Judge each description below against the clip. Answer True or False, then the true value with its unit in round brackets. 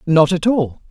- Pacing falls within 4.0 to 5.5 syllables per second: True (4.3 syllables/s)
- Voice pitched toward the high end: False (175 Hz)